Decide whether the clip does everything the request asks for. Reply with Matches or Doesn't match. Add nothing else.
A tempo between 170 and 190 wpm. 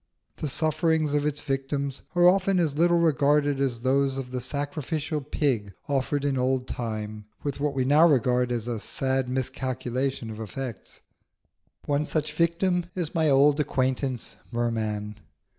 Doesn't match